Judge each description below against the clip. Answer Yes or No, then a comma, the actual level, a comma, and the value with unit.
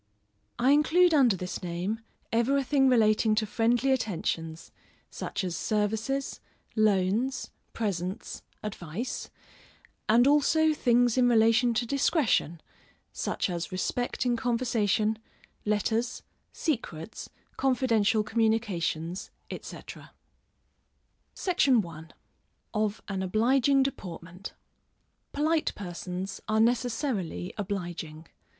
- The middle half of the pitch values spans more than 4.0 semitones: Yes, average, 5.0 semitones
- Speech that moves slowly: Yes, slow, 95 wpm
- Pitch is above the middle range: Yes, high, 220 Hz